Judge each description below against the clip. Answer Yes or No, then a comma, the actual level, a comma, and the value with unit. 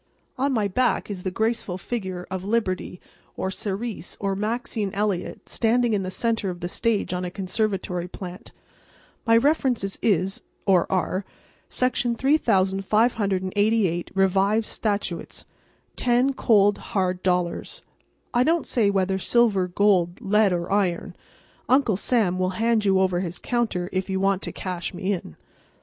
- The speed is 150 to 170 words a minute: No, slow, 135 wpm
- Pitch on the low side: No, high, 195 Hz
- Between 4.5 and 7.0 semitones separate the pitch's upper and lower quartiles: No, average, 3.6 semitones